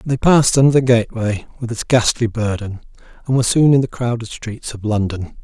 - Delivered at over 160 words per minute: Yes, average, 200 wpm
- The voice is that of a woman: No, male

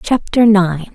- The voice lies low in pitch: No, high, 200 Hz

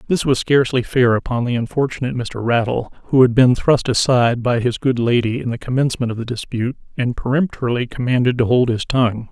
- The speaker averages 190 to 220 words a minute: Yes, average, 200 wpm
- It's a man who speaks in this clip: Yes, male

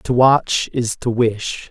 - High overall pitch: No, low, 120 Hz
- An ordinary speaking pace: Yes, average, 175 wpm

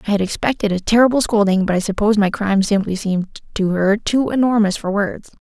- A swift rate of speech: Yes, fast, 210 wpm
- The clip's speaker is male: No, female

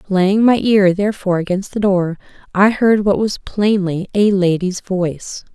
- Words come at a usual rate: Yes, average, 160 wpm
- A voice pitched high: Yes, high, 195 Hz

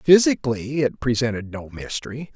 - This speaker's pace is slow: Yes, slow, 125 wpm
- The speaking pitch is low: Yes, low, 125 Hz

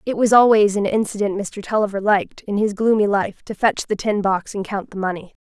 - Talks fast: Yes, fast, 230 wpm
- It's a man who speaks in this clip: No, female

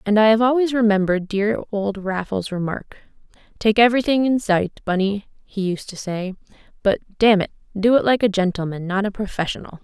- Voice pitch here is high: Yes, high, 205 Hz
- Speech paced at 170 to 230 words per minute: Yes, average, 175 wpm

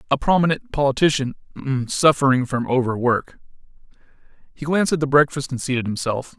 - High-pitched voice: No, low, 135 Hz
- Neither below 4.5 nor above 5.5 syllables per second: No, 6.2 syllables/s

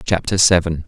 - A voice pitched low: Yes, very low, 85 Hz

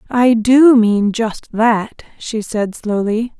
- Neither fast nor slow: No, slow, 70 wpm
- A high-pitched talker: Yes, high, 225 Hz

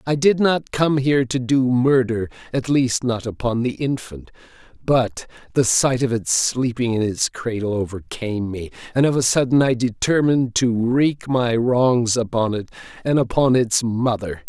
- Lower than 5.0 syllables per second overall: Yes, 4.5 syllables/s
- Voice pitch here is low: Yes, low, 125 Hz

